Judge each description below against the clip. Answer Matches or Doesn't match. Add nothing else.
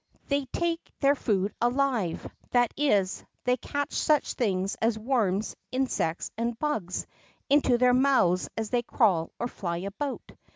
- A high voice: Matches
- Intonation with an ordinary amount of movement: Doesn't match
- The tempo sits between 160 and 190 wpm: Doesn't match